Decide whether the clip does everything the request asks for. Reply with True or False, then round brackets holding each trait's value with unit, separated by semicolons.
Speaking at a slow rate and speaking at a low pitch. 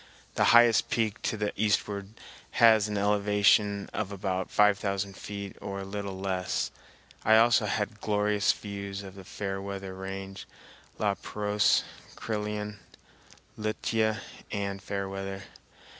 True (125 wpm; 100 Hz)